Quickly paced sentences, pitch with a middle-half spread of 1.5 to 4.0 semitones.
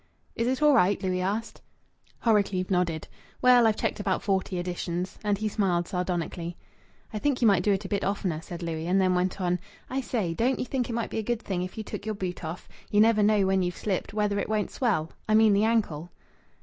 Yes: fast, 230 wpm; average, 3.4 semitones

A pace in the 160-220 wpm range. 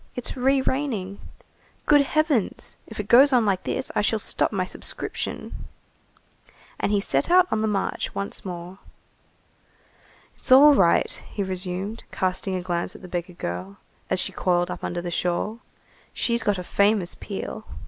Yes: average, 165 wpm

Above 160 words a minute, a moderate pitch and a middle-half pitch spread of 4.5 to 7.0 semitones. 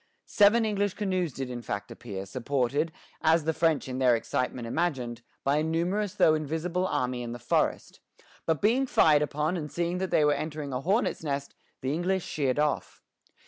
Yes: average, 185 wpm; medium, 155 Hz; average, 5.2 semitones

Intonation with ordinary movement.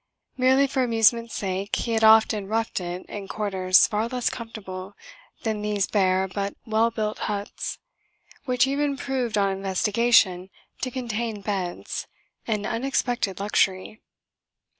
Yes: average, 3.2 semitones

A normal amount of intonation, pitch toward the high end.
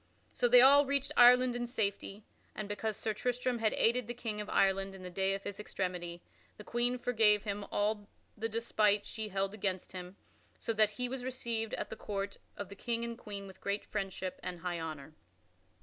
Yes: average, 3.3 semitones; high, 210 Hz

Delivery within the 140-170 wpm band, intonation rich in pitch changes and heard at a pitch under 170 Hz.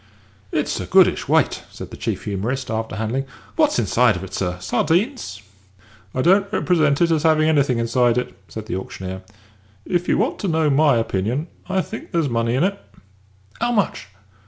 No: average, 180 wpm; wide, 7.2 semitones; low, 135 Hz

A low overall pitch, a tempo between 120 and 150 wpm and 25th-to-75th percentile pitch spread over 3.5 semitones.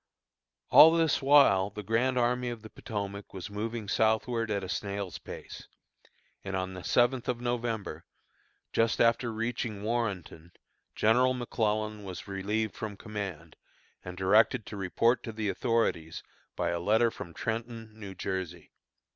No: low, 110 Hz; average, 140 wpm; average, 3.2 semitones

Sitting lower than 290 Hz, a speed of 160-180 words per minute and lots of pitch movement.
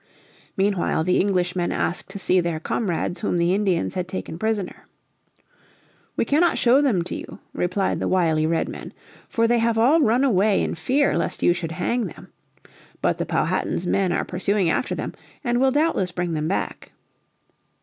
No: high, 190 Hz; average, 170 wpm; average, 4.6 semitones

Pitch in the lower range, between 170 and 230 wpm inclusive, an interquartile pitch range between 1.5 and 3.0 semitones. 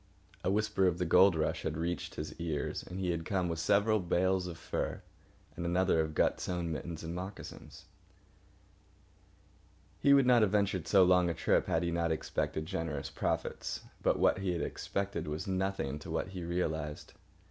Yes: very low, 90 Hz; average, 180 wpm; average, 2.7 semitones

